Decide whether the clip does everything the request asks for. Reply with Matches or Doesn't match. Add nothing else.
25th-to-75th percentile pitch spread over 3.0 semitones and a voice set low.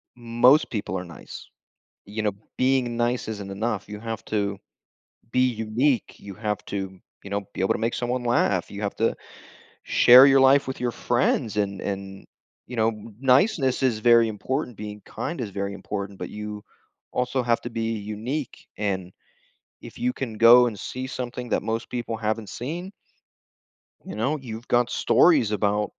Matches